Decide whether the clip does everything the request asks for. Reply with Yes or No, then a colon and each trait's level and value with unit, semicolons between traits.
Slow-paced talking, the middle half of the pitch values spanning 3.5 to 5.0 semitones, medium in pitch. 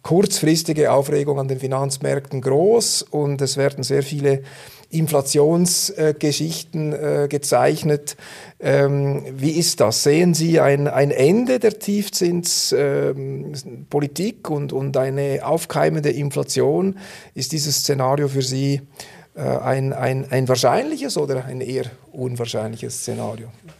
No: slow, 100 wpm; average, 2.8 semitones; medium, 145 Hz